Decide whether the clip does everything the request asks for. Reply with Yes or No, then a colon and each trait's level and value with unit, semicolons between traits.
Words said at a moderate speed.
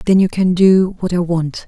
No: fast, 250 wpm